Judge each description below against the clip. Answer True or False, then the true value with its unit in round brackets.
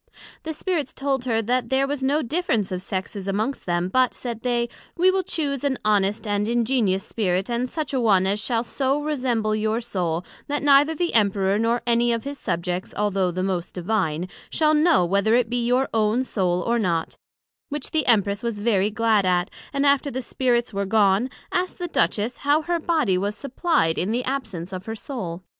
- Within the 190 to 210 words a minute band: True (195 wpm)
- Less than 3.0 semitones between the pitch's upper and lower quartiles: False (5.5 semitones)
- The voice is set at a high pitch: True (230 Hz)